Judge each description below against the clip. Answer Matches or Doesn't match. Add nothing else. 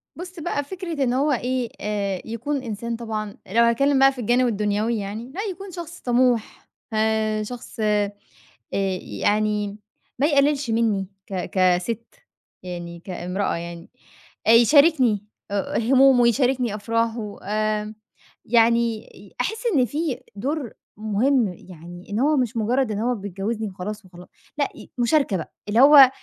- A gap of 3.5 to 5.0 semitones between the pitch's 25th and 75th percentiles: Matches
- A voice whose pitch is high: Matches